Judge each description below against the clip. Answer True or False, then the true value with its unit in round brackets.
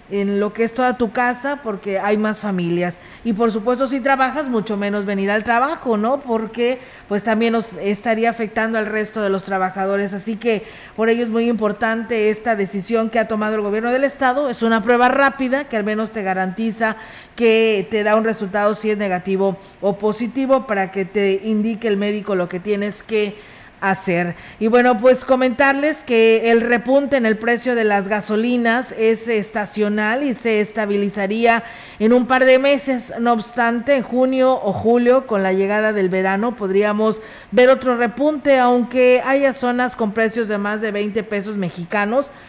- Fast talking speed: False (180 wpm)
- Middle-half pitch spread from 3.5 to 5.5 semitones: False (3.0 semitones)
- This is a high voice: True (225 Hz)